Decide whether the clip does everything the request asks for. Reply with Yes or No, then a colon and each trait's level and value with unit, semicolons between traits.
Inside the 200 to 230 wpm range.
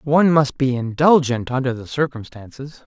No: average, 145 wpm